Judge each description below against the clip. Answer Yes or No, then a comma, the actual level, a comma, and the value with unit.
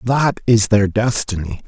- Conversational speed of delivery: Yes, average, 145 wpm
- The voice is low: Yes, low, 110 Hz